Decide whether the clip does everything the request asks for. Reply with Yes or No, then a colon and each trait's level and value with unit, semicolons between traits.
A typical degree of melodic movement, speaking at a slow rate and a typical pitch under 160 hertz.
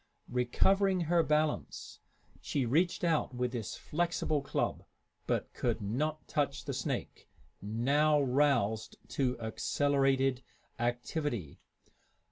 Yes: average, 4.0 semitones; slow, 100 wpm; medium, 140 Hz